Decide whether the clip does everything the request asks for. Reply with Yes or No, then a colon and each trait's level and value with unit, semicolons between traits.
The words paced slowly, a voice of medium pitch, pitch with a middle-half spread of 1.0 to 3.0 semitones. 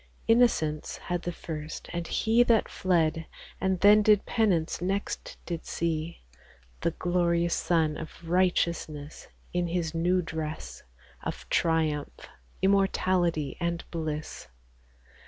Yes: slow, 115 wpm; medium, 170 Hz; narrow, 2.6 semitones